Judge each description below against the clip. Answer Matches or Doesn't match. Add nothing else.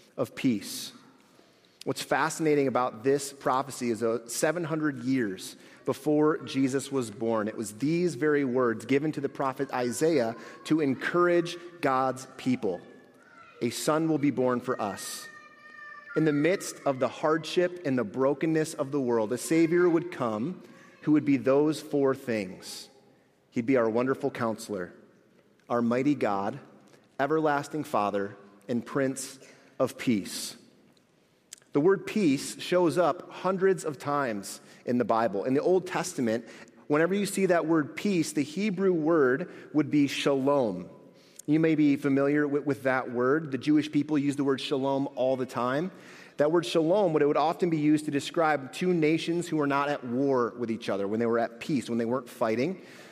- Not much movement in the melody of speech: Doesn't match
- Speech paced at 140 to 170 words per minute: Matches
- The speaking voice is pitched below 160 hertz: Matches